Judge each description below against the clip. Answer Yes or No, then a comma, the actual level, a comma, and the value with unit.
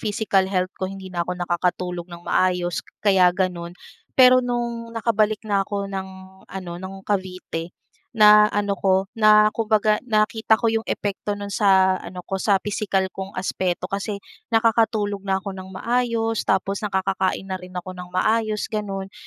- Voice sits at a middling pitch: No, high, 195 Hz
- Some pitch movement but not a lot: No, narrow, 2.3 semitones